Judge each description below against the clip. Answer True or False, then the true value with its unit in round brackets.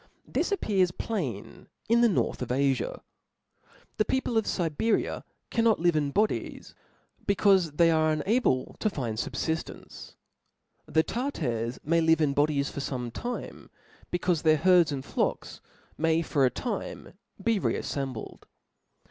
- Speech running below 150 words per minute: True (140 wpm)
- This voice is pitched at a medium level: True (160 Hz)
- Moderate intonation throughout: False (6.4 semitones)